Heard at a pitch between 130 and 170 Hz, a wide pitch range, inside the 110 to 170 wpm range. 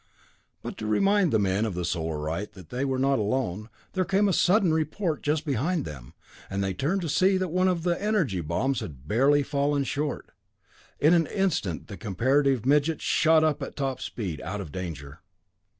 No: low, 135 Hz; wide, 8.9 semitones; average, 190 wpm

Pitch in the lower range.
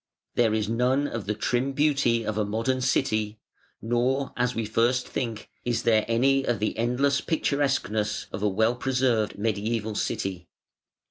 Yes: low, 115 Hz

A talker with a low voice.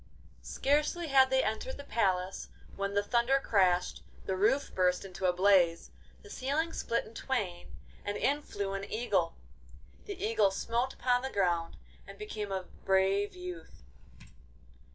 No: high, 205 Hz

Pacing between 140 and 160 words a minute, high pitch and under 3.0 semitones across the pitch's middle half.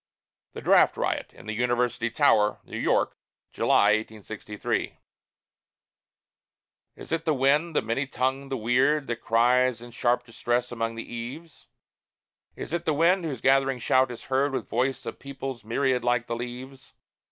No: average, 155 wpm; low, 125 Hz; narrow, 2.6 semitones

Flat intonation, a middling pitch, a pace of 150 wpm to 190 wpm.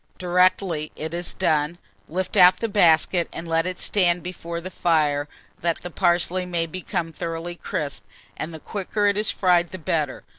Yes: narrow, 2.0 semitones; medium, 175 Hz; average, 175 wpm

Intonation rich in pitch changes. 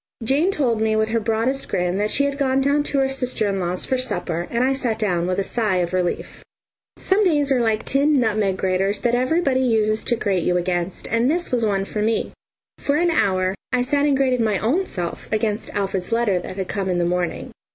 Yes: wide, 5.7 semitones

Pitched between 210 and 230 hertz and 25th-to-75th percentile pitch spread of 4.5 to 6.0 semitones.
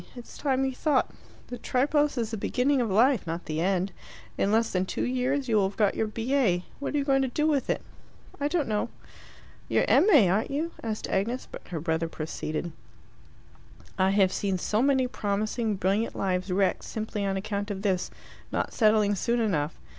Yes: high, 215 Hz; average, 5.2 semitones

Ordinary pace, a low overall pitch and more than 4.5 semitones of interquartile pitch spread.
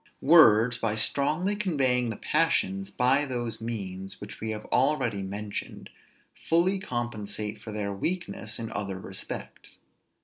No: slow, 130 wpm; low, 115 Hz; average, 5.3 semitones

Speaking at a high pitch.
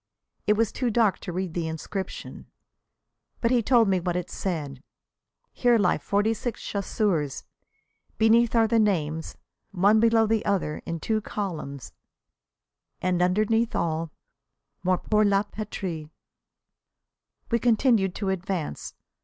Yes: high, 200 Hz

